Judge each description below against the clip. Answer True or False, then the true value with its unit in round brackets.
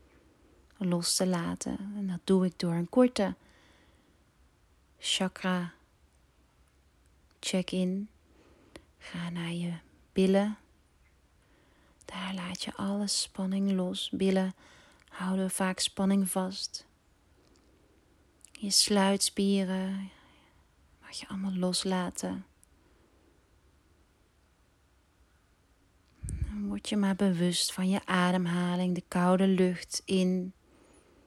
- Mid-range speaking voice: True (180 Hz)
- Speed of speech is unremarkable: False (85 wpm)